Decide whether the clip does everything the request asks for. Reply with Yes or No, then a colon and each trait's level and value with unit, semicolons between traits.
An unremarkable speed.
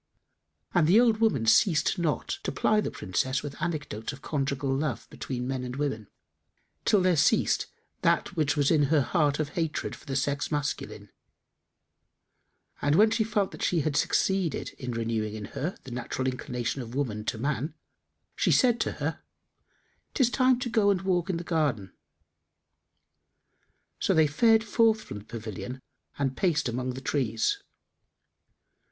Yes: average, 160 wpm